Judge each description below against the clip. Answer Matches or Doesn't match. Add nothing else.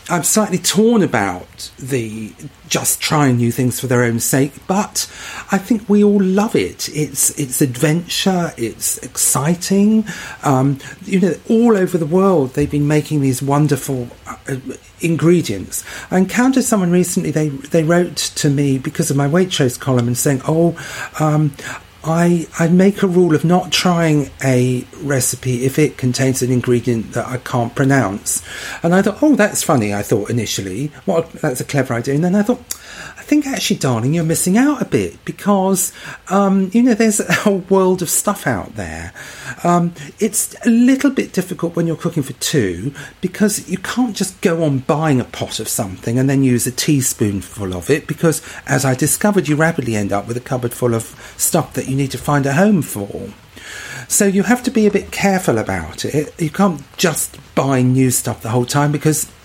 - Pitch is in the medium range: Matches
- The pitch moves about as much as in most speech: Doesn't match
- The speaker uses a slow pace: Doesn't match